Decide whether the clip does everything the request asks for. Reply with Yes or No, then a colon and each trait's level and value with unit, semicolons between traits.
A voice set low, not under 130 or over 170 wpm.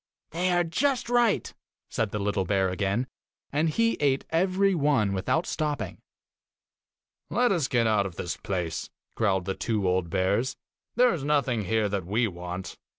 Yes: low, 115 Hz; average, 160 wpm